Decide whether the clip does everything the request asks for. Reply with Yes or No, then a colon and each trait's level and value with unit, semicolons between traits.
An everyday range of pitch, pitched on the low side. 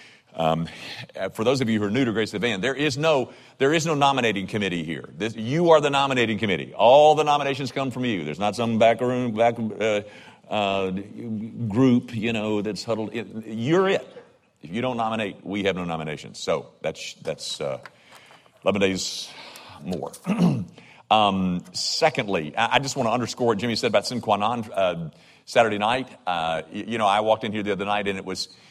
Yes: average, 4.4 semitones; low, 110 Hz